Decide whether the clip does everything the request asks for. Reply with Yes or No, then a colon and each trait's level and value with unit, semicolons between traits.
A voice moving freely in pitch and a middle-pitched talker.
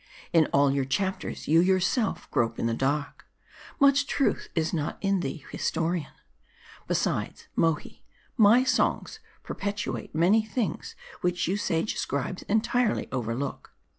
Yes: wide, 6.6 semitones; medium, 175 Hz